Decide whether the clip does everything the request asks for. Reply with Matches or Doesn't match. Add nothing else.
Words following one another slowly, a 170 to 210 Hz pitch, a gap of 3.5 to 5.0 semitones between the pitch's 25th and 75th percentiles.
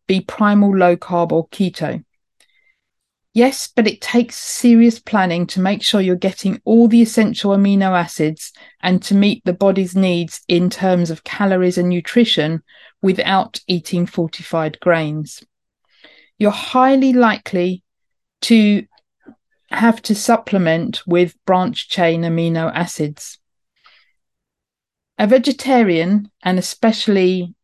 Matches